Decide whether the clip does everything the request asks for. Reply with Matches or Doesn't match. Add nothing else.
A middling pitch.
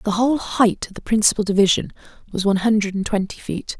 Doesn't match